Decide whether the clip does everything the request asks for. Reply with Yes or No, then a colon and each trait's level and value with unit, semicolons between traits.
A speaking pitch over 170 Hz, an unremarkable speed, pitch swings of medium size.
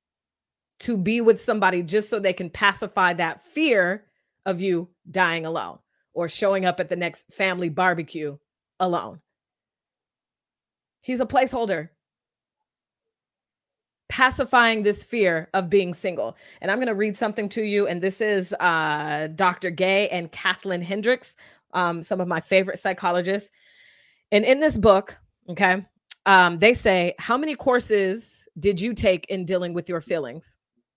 Yes: high, 190 Hz; average, 145 wpm; average, 3.4 semitones